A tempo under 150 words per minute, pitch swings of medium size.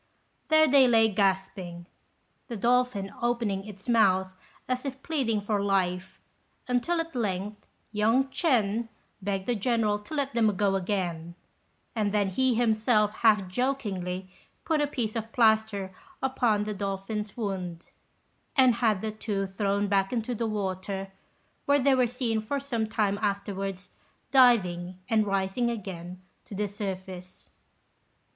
Yes: average, 140 wpm; average, 3.7 semitones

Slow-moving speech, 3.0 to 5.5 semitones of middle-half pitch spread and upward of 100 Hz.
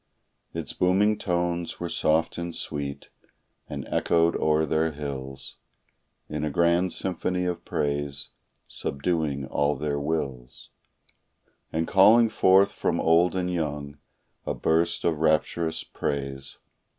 No: slow, 120 wpm; average, 3.4 semitones; very low, 80 Hz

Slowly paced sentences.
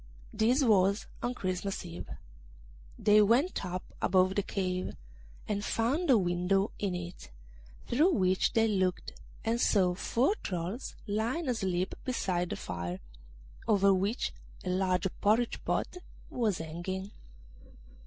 Yes: slow, 125 wpm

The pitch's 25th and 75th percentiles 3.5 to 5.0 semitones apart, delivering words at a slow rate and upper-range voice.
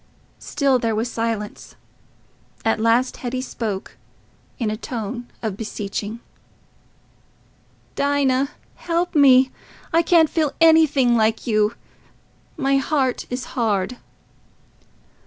Yes: average, 3.9 semitones; slow, 100 wpm; very high, 250 Hz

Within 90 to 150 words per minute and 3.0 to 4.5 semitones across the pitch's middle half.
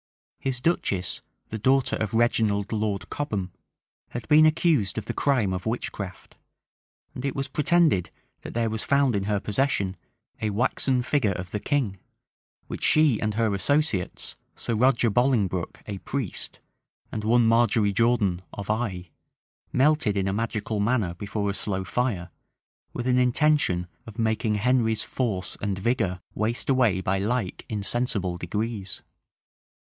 Yes: average, 145 wpm; average, 4.1 semitones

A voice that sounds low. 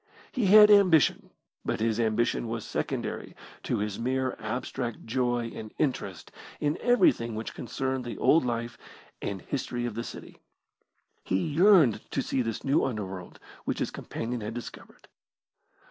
Yes: low, 120 Hz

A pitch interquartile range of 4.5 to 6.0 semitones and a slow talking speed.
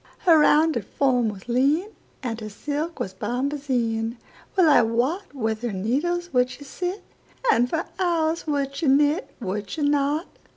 Yes: average, 5.2 semitones; slow, 130 wpm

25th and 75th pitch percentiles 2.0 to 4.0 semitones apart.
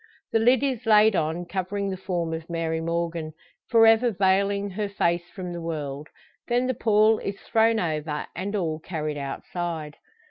No: average, 4.6 semitones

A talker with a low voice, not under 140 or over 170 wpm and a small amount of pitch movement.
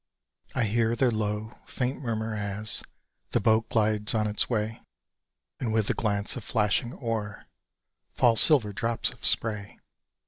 Yes: low, 110 Hz; average, 145 wpm; narrow, 1.8 semitones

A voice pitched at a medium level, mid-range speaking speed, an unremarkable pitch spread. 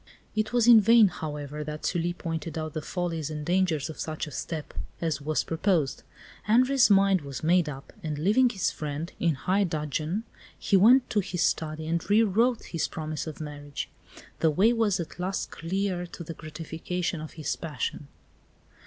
Yes: medium, 165 Hz; average, 180 wpm; average, 4.1 semitones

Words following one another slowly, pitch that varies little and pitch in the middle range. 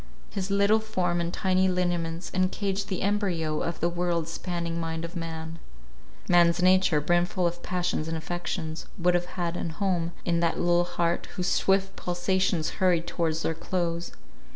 No: average, 160 wpm; narrow, 1.7 semitones; medium, 175 Hz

